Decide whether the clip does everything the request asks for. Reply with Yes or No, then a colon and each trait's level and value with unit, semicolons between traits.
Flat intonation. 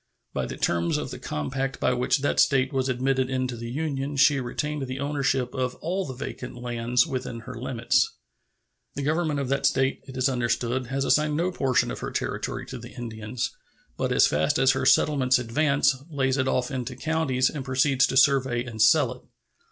Yes: narrow, 1.9 semitones